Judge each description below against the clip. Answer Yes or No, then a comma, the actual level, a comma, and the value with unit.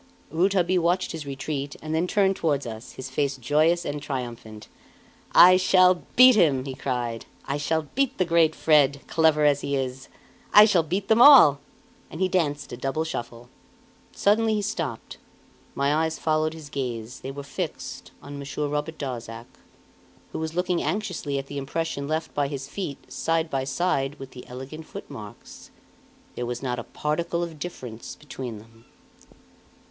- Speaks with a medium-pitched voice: Yes, medium, 145 Hz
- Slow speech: No, average, 165 wpm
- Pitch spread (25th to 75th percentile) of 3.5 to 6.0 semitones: Yes, average, 4.0 semitones